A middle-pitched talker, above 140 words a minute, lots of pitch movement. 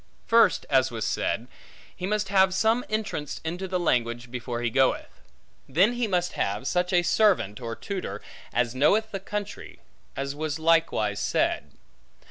Yes: medium, 165 Hz; average, 155 wpm; wide, 8.2 semitones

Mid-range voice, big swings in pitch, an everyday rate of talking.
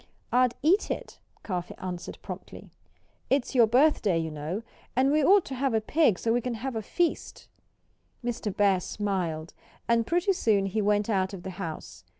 No: high, 220 Hz; wide, 5.7 semitones; average, 180 wpm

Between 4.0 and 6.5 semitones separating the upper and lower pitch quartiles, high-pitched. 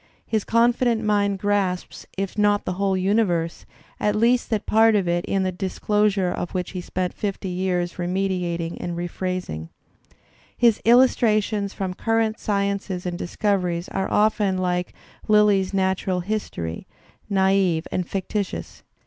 No: narrow, 2.6 semitones; high, 195 Hz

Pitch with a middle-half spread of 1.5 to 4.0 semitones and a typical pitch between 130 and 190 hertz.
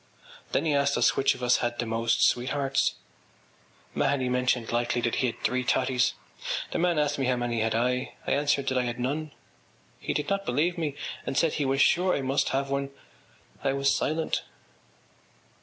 Yes: average, 2.7 semitones; low, 135 Hz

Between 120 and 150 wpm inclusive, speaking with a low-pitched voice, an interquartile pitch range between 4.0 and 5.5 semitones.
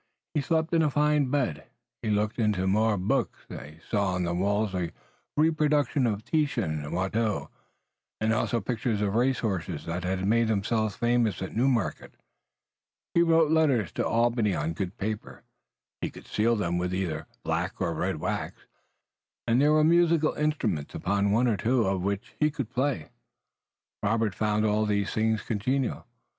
No: average, 165 wpm; low, 110 Hz; average, 5.2 semitones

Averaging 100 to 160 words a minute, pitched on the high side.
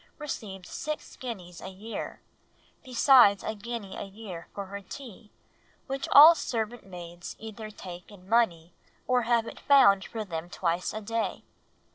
Yes: average, 150 wpm; high, 215 Hz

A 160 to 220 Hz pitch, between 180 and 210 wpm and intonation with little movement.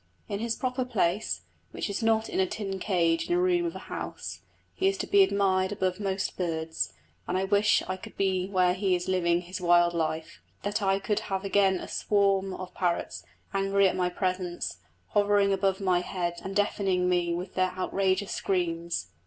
Yes: high, 190 Hz; average, 195 wpm; narrow, 2.2 semitones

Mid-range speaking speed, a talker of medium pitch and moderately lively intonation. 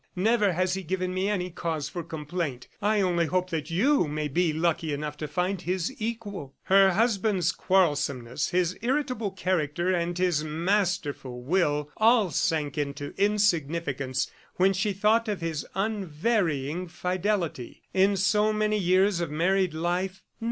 Yes: average, 145 wpm; medium, 180 Hz; average, 4.0 semitones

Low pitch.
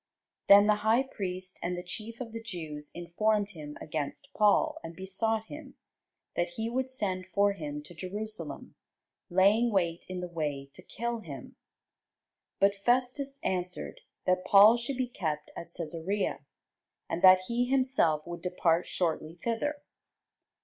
No: high, 195 Hz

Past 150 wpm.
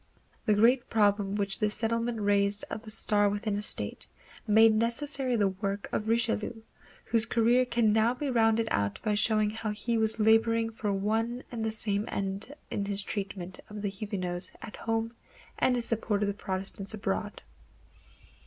Yes: average, 170 wpm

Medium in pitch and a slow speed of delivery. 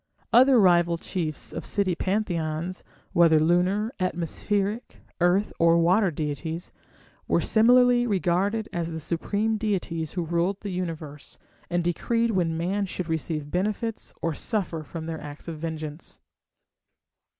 Yes: medium, 175 Hz; slow, 130 wpm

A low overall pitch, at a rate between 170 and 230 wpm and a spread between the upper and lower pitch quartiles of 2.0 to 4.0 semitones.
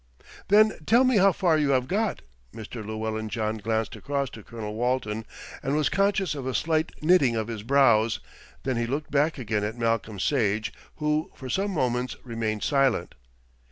No: low, 125 Hz; average, 175 wpm; wide, 5.6 semitones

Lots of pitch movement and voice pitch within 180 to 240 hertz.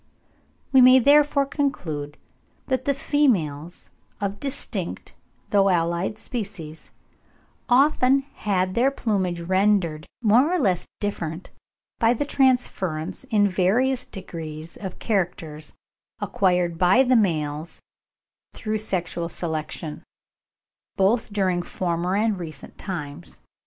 Yes: wide, 6.3 semitones; high, 190 Hz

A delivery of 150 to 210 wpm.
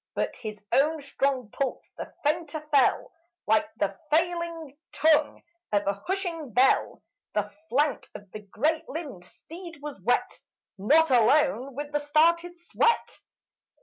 No: slow, 135 wpm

